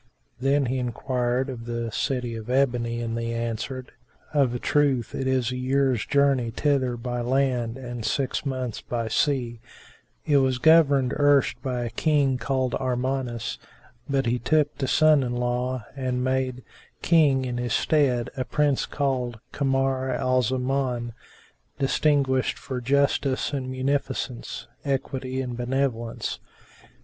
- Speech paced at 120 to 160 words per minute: Yes, average, 140 wpm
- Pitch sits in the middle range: No, low, 130 Hz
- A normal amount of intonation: No, narrow, 2.0 semitones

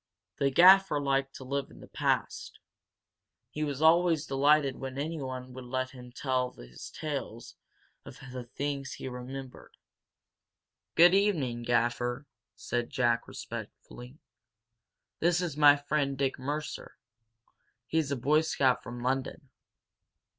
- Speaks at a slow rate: Yes, slow, 125 wpm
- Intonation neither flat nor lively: Yes, average, 3.0 semitones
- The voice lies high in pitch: No, low, 135 Hz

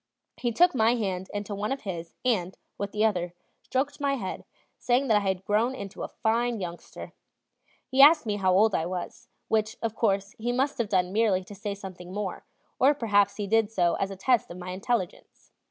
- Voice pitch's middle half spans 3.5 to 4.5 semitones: Yes, average, 3.8 semitones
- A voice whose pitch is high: Yes, high, 205 Hz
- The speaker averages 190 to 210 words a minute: Yes, fast, 205 wpm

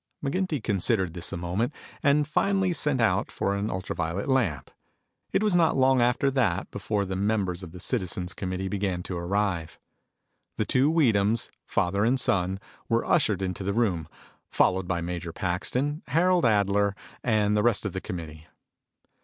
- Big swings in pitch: Yes, wide, 5.7 semitones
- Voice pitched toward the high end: No, low, 100 Hz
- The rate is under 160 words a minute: No, average, 165 wpm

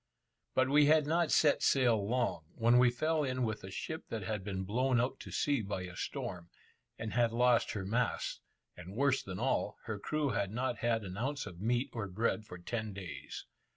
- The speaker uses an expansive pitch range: No, average, 4.6 semitones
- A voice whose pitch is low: Yes, low, 115 Hz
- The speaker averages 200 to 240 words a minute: Yes, fast, 205 wpm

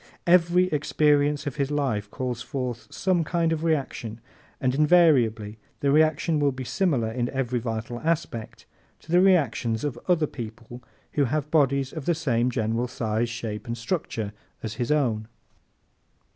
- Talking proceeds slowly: No, average, 155 wpm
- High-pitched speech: No, low, 135 Hz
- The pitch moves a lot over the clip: No, average, 4.9 semitones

